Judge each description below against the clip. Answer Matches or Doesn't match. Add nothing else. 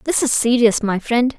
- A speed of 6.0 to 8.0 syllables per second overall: Doesn't match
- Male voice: Doesn't match